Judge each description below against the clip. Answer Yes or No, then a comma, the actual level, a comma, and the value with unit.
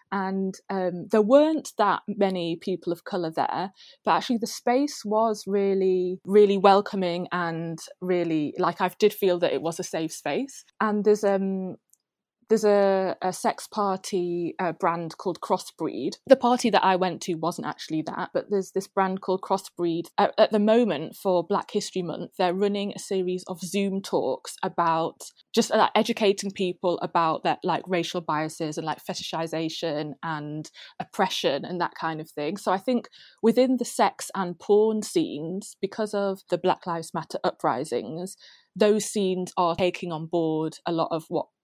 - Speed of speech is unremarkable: Yes, average, 170 wpm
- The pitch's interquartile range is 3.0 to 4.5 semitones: Yes, average, 3.3 semitones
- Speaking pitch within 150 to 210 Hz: Yes, medium, 185 Hz